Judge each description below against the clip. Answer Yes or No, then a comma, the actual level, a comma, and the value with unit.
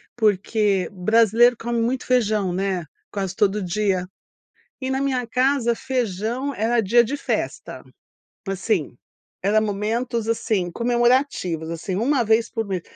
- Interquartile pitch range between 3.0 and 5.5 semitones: Yes, average, 3.7 semitones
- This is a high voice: Yes, high, 220 Hz